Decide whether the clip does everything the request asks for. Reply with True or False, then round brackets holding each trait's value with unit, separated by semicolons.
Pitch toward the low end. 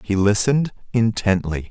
True (105 Hz)